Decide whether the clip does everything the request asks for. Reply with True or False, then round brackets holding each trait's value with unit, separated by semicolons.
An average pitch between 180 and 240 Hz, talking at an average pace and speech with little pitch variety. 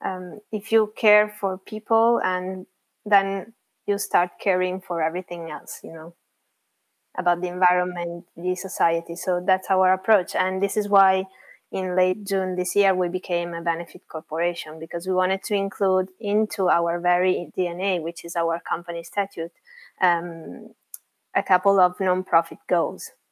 True (185 Hz; 150 wpm; 2.2 semitones)